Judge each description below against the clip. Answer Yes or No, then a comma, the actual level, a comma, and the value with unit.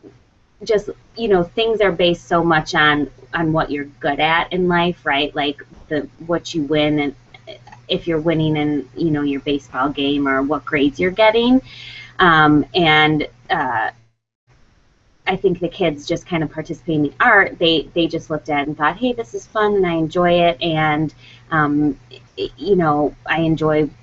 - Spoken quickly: No, average, 185 wpm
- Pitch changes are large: No, average, 3.1 semitones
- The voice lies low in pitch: No, medium, 155 Hz